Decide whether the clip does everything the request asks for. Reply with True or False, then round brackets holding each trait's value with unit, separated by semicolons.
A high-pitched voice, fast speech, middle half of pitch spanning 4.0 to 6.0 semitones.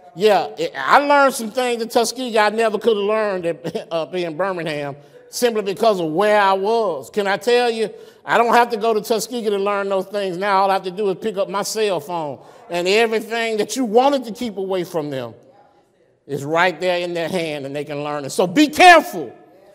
True (210 Hz; 220 wpm; 4.4 semitones)